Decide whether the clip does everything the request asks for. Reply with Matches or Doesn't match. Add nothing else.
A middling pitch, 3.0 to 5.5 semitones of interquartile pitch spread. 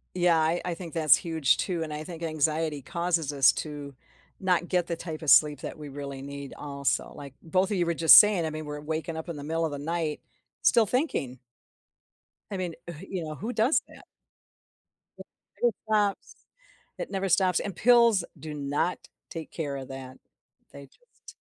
Matches